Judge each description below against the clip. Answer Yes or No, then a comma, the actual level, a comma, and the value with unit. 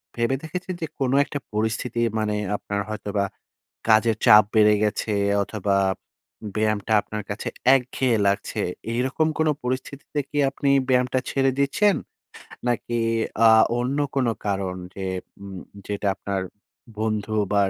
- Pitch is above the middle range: No, low, 110 Hz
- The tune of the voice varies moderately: Yes, average, 4.1 semitones